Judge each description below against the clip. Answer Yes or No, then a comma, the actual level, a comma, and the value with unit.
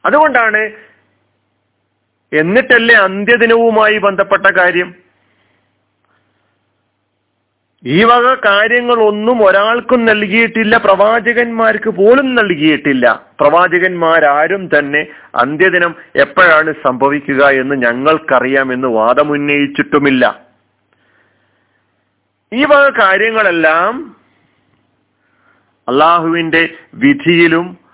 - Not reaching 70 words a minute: Yes, slow, 60 wpm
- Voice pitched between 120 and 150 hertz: No, medium, 165 Hz